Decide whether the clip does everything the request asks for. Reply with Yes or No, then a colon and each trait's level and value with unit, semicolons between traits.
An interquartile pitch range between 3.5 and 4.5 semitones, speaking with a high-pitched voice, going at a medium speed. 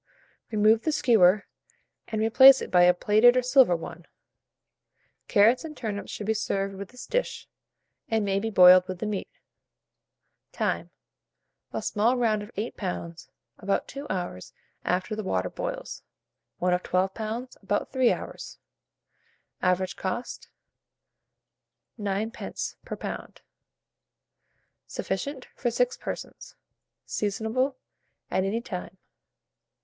No: average, 4.2 semitones; high, 210 Hz; slow, 125 wpm